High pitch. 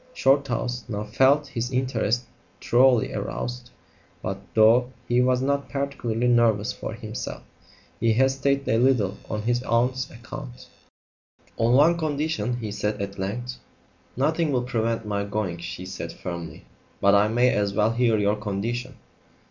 No: low, 120 Hz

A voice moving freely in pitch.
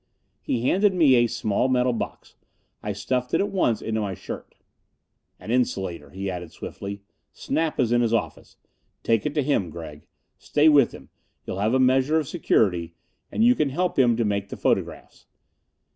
Yes: wide, 5.8 semitones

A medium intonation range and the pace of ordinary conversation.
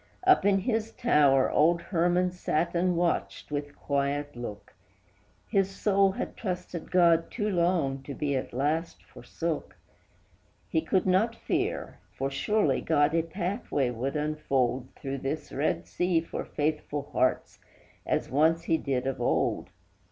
Yes: average, 4.6 semitones; average, 145 wpm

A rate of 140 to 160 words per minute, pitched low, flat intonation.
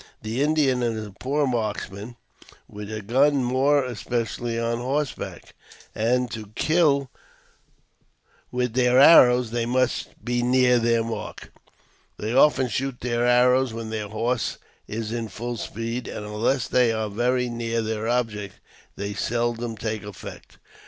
Yes: average, 145 wpm; low, 120 Hz; narrow, 2.2 semitones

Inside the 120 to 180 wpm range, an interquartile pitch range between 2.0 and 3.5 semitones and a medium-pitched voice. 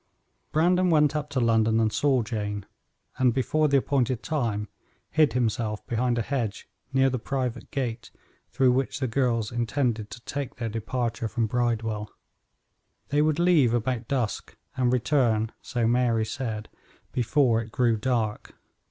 No: average, 150 wpm; average, 3.0 semitones; low, 120 Hz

